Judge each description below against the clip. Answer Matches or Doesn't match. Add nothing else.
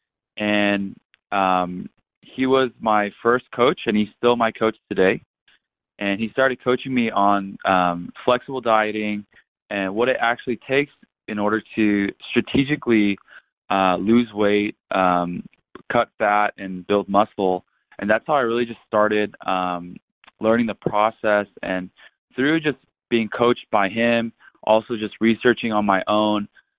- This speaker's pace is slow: Doesn't match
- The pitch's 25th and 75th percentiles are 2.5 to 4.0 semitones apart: Matches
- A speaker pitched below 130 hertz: Matches